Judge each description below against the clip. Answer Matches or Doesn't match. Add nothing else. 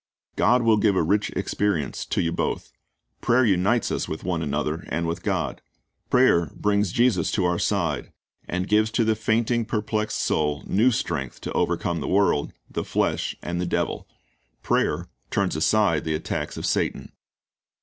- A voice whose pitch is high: Doesn't match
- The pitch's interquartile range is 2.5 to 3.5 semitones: Doesn't match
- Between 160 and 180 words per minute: Matches